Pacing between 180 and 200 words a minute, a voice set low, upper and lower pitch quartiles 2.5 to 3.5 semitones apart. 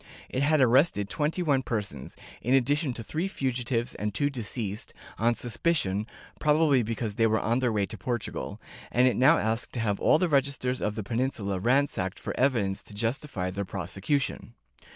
No: average, 190 wpm; low, 120 Hz; average, 4.8 semitones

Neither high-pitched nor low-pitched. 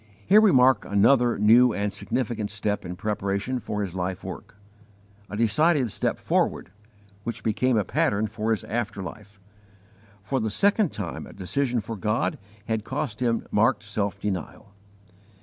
No: low, 110 Hz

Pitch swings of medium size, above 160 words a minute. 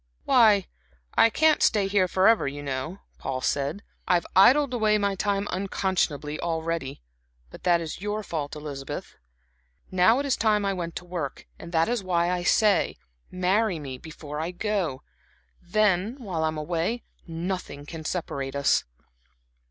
No: average, 4.6 semitones; average, 155 wpm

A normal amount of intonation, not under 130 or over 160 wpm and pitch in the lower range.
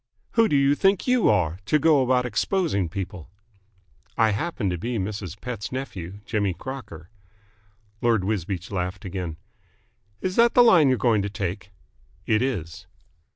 No: wide, 6.6 semitones; average, 155 wpm; low, 110 Hz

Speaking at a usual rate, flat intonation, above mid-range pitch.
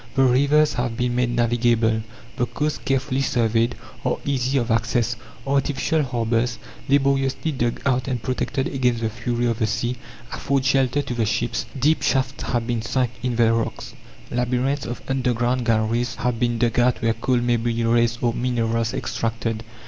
No: average, 170 wpm; narrow, 2.1 semitones; low, 120 Hz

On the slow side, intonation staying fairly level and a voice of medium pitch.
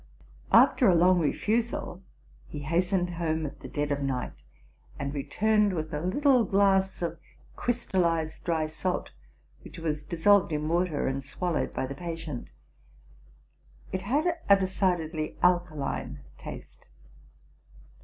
No: slow, 125 wpm; average, 3.7 semitones; medium, 170 Hz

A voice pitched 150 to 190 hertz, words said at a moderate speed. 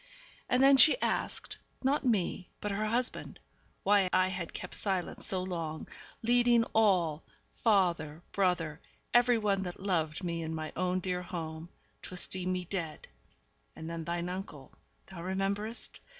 Yes: medium, 185 Hz; average, 150 wpm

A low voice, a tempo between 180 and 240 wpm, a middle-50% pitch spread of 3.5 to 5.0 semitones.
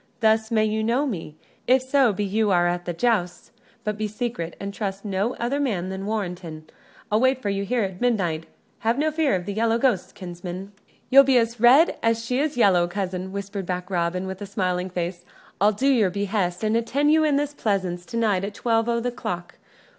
No: high, 205 Hz; fast, 205 wpm; average, 4.4 semitones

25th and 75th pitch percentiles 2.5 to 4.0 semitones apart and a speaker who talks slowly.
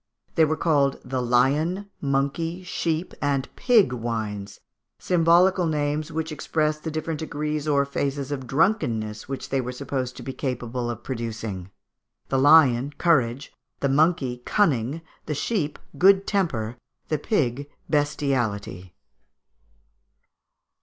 No: average, 4.4 semitones; slow, 125 wpm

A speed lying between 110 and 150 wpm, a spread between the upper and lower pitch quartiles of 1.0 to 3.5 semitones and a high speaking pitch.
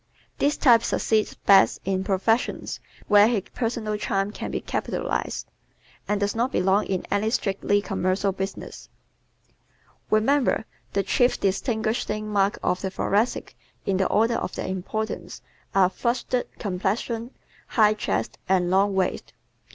Yes: slow, 135 wpm; narrow, 2.6 semitones; high, 205 Hz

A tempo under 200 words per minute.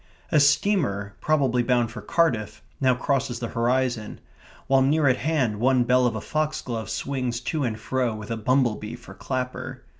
Yes: average, 175 wpm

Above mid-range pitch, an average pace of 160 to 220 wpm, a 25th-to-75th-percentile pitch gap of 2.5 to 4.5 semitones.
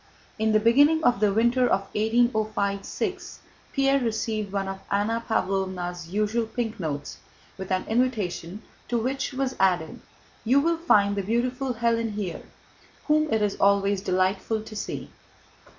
No: high, 215 Hz; average, 150 wpm; average, 3.6 semitones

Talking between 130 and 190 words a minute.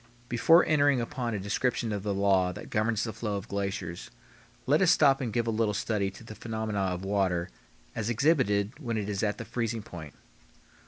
No: average, 200 wpm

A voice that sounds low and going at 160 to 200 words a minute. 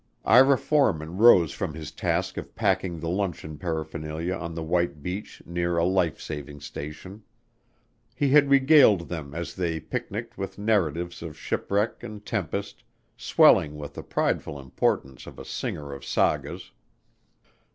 No: very low, 85 Hz; average, 145 wpm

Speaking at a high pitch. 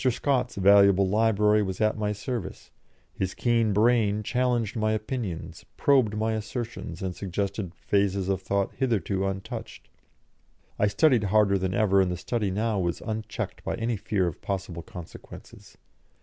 No: low, 105 Hz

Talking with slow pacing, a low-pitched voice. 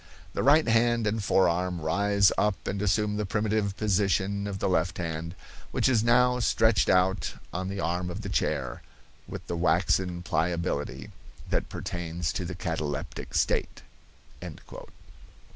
No: average, 145 wpm; very low, 95 Hz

